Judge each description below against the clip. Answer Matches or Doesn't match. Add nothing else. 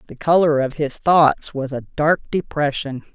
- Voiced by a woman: Matches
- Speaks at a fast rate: Doesn't match